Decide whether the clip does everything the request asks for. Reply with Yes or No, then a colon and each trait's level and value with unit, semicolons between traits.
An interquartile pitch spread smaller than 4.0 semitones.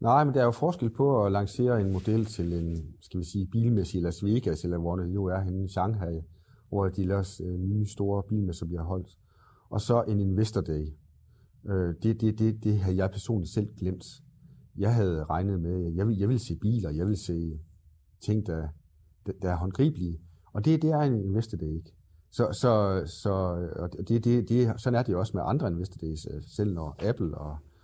No: average, 4.3 semitones